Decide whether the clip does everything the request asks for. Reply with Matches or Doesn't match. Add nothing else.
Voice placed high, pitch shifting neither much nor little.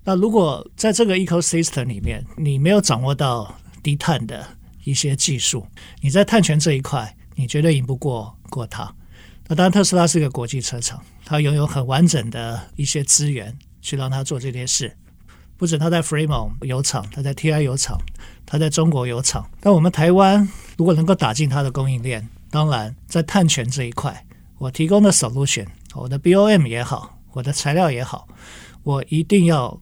Doesn't match